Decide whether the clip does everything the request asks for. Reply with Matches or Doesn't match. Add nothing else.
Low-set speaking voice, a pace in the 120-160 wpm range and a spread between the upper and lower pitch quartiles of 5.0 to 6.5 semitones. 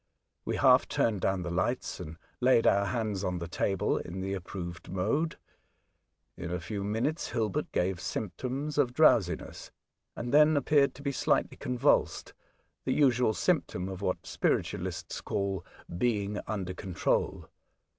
Matches